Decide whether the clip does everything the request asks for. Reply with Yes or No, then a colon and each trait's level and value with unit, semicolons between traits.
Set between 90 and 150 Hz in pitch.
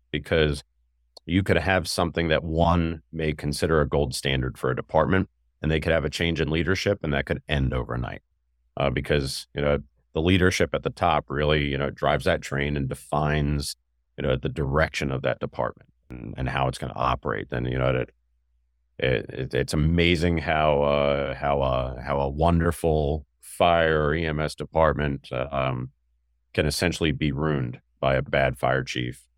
No: very low, 75 Hz